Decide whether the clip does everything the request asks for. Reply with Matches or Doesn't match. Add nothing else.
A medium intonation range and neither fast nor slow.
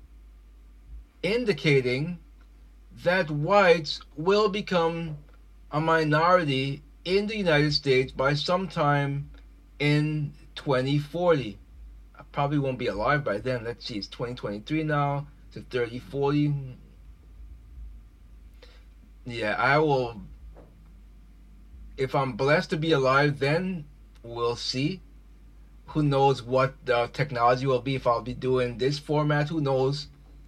Doesn't match